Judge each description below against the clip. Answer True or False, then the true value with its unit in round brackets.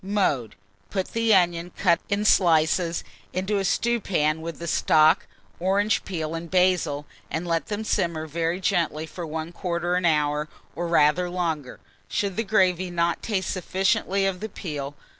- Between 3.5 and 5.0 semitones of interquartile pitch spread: False (3.0 semitones)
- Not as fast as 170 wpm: True (150 wpm)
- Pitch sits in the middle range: True (175 Hz)